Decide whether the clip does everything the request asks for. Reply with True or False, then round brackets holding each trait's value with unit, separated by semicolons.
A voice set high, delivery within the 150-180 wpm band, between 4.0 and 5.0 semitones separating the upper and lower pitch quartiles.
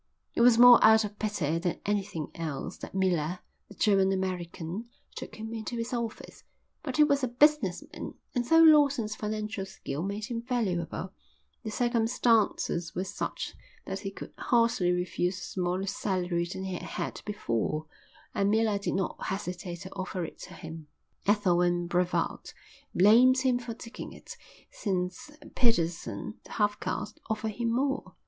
True (200 Hz; 160 wpm; 4.5 semitones)